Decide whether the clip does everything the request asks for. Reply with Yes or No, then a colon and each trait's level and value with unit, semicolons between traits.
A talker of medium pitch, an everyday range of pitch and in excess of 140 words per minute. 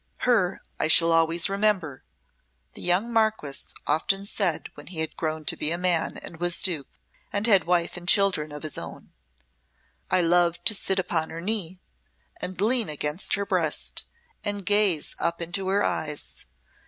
Yes: medium, 175 Hz; average, 3.6 semitones; average, 165 wpm